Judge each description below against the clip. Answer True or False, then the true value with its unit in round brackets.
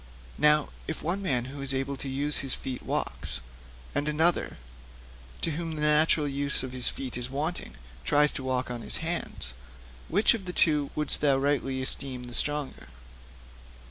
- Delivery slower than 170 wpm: False (175 wpm)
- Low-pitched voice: False (145 Hz)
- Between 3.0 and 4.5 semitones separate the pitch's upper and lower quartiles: False (2.5 semitones)